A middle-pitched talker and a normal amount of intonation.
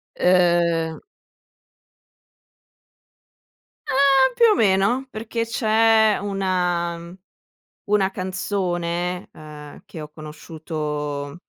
Yes: medium, 180 Hz; average, 4.8 semitones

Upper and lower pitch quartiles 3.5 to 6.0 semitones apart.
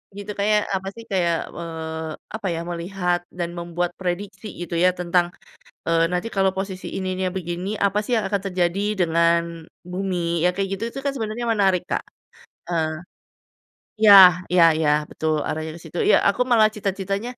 No: average, 2.7 semitones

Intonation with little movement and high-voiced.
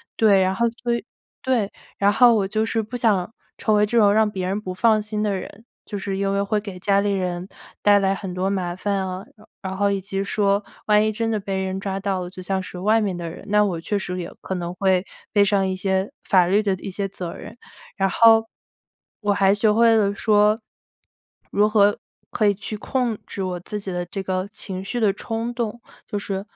Yes: narrow, 2.0 semitones; high, 200 Hz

